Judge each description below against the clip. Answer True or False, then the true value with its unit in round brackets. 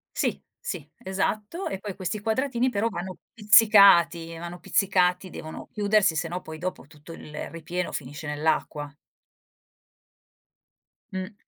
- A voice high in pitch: False (180 Hz)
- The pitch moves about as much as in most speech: True (4.0 semitones)